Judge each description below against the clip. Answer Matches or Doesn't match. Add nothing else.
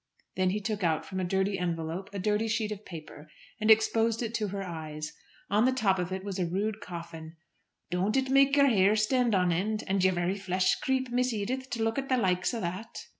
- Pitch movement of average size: Matches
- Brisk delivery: Matches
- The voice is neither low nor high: Doesn't match